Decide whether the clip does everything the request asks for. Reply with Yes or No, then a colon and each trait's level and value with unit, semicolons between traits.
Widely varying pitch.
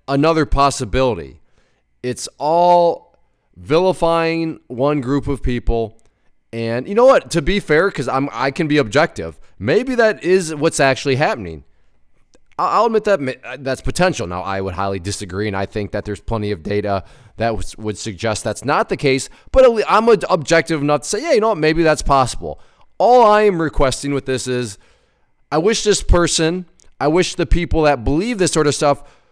Yes: wide, 6.7 semitones